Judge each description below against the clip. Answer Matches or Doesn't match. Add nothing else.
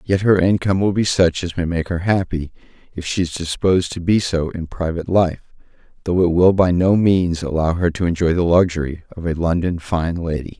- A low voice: Matches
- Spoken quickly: Matches